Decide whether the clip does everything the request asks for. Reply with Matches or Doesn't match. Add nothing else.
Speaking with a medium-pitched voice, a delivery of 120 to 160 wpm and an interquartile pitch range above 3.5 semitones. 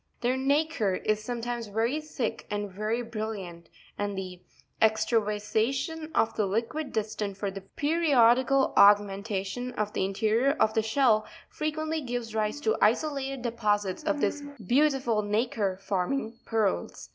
Doesn't match